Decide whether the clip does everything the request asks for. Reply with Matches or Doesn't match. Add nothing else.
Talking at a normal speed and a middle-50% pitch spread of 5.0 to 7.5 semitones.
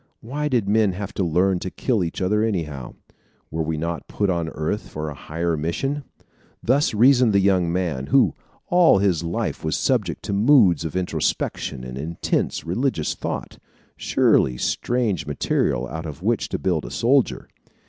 Matches